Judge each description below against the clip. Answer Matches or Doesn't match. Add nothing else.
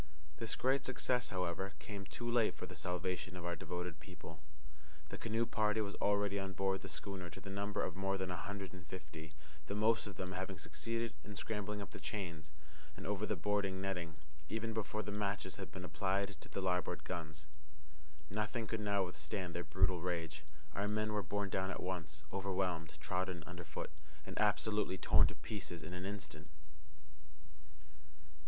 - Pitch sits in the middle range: Doesn't match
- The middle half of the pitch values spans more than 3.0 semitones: Doesn't match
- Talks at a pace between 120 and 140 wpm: Doesn't match